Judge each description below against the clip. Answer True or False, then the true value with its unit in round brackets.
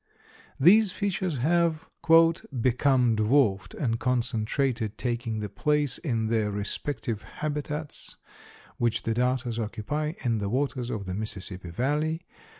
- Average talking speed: False (120 wpm)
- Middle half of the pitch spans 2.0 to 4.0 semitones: False (5.1 semitones)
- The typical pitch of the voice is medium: False (125 Hz)